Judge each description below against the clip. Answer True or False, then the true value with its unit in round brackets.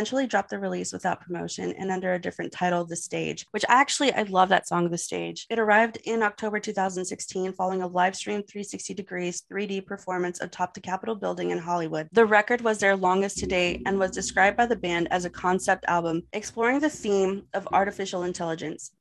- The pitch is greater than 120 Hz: True (190 Hz)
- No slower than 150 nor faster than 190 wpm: False (200 wpm)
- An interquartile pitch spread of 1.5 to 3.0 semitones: True (2.7 semitones)